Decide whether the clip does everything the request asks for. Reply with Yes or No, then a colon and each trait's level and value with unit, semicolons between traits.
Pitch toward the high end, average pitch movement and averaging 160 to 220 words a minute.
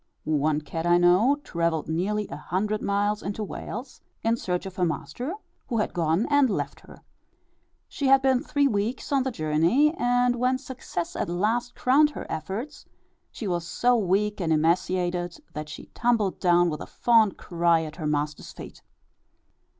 No: high, 200 Hz; wide, 6.3 semitones; average, 170 wpm